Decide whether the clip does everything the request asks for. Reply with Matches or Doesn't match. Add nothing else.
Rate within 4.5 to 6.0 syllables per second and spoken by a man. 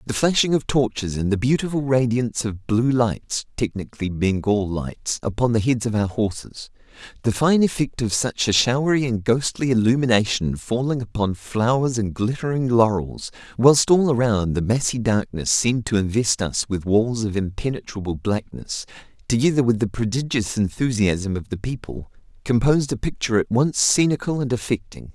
Matches